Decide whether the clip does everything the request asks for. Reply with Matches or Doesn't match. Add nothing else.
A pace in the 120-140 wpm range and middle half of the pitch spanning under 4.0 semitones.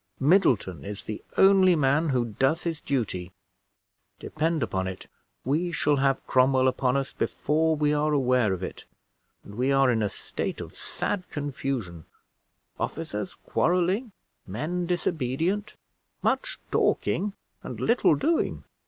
Doesn't match